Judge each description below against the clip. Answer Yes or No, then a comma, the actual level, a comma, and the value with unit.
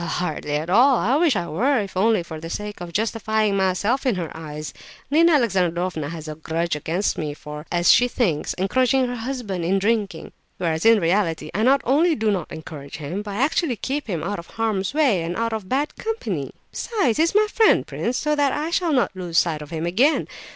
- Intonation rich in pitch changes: Yes, wide, 7.3 semitones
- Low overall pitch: No, high, 200 Hz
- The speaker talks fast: Yes, fast, 215 wpm